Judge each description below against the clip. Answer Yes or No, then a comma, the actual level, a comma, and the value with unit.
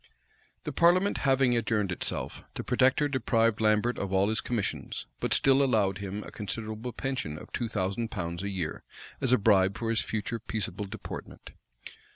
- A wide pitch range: No, average, 3.7 semitones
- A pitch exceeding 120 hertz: No, low, 110 Hz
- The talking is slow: No, average, 170 wpm